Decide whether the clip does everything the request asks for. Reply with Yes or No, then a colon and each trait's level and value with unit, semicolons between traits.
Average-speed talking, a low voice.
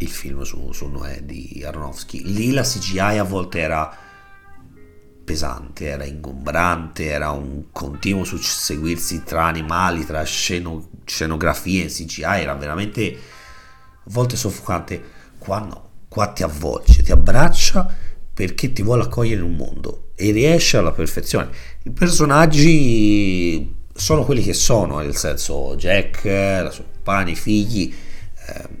Yes: average, 135 wpm; very low, 85 Hz